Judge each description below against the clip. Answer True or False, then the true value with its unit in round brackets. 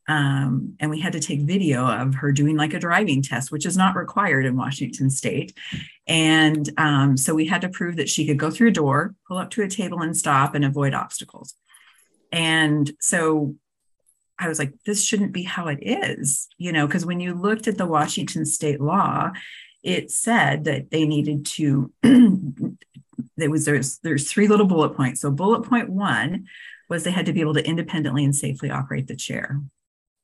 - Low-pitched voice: False (155 Hz)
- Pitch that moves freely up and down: False (3.9 semitones)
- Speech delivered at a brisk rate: False (195 wpm)